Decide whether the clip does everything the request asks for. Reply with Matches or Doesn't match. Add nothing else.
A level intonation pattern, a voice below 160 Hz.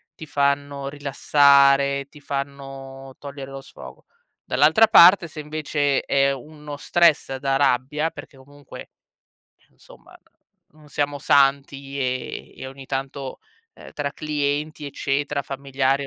Matches